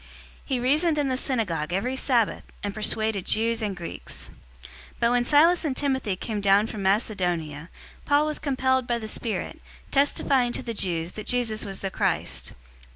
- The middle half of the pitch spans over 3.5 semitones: Yes, average, 5.0 semitones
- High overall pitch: Yes, high, 225 Hz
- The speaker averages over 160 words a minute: Yes, average, 175 wpm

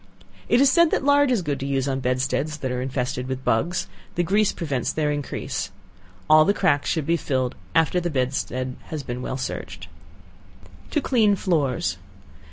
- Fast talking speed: No, average, 175 wpm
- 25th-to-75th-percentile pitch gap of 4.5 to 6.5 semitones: Yes, wide, 5.5 semitones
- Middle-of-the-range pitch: Yes, medium, 145 Hz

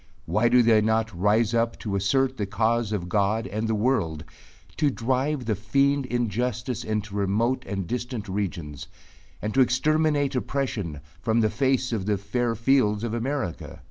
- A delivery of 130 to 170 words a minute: Yes, average, 165 wpm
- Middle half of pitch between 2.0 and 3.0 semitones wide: No, average, 3.6 semitones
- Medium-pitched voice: No, low, 115 Hz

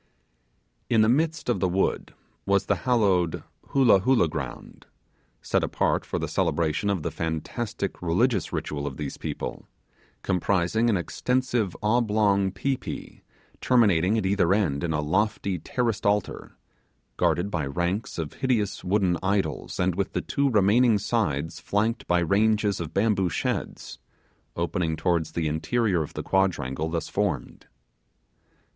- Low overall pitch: Yes, very low, 95 Hz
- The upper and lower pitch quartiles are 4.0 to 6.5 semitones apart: Yes, average, 4.5 semitones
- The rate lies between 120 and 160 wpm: Yes, average, 140 wpm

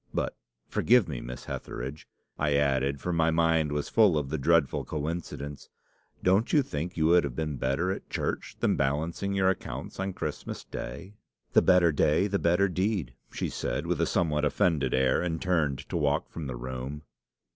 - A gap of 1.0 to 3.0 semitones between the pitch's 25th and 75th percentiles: No, average, 4.2 semitones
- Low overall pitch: Yes, very low, 80 Hz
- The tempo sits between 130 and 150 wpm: No, average, 180 wpm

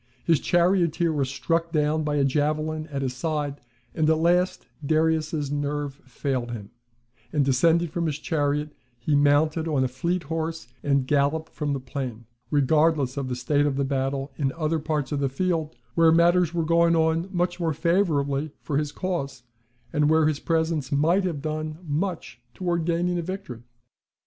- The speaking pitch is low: No, medium, 155 Hz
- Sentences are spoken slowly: No, average, 175 wpm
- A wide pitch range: No, average, 2.8 semitones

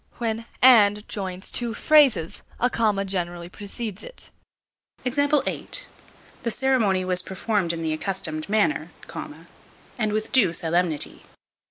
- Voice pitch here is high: Yes, high, 205 Hz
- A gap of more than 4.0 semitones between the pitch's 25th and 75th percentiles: Yes, average, 4.5 semitones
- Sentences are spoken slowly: Yes, slow, 115 wpm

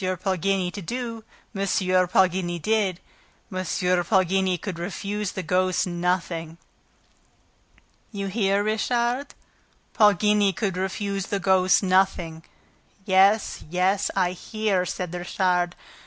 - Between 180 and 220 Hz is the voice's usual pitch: Yes, high, 190 Hz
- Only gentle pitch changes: Yes, narrow, 2.1 semitones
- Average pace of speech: No, slow, 105 wpm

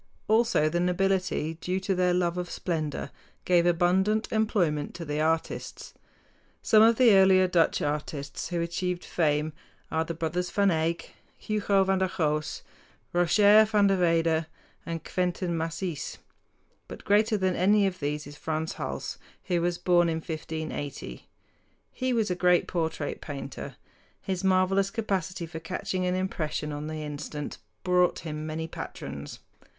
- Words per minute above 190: No, average, 150 wpm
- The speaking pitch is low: No, medium, 175 Hz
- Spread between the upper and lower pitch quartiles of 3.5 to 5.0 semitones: No, average, 3.1 semitones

